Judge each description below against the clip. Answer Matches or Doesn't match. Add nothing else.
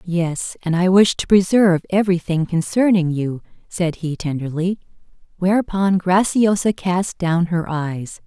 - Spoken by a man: Doesn't match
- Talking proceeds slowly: Matches